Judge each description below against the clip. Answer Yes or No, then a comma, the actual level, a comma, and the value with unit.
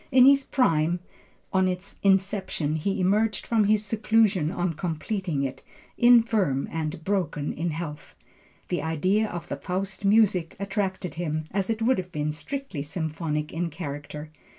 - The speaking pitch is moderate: Yes, medium, 180 Hz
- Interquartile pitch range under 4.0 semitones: No, average, 4.9 semitones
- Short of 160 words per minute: Yes, average, 150 wpm